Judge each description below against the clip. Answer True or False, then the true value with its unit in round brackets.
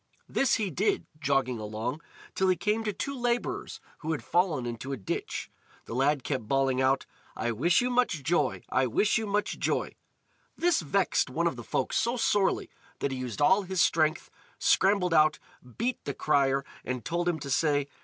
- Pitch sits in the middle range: True (155 Hz)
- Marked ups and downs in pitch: True (6.9 semitones)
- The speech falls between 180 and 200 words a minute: True (185 wpm)